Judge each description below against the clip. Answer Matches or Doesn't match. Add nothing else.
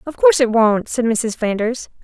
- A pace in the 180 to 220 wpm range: Matches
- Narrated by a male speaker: Doesn't match